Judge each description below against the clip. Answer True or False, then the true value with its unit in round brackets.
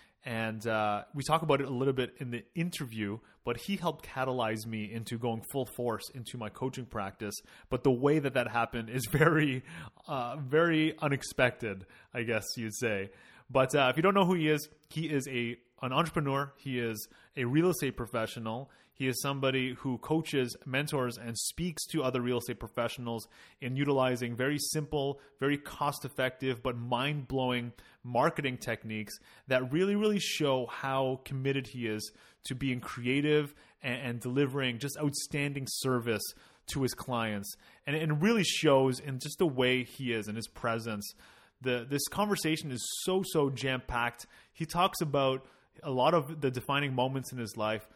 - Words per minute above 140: True (170 wpm)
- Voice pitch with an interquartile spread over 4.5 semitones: False (3.5 semitones)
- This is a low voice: True (130 Hz)